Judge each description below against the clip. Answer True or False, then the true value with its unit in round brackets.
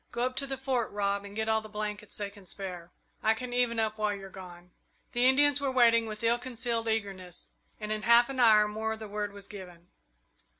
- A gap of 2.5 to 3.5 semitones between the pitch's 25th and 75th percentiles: True (2.9 semitones)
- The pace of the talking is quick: True (220 wpm)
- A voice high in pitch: True (220 Hz)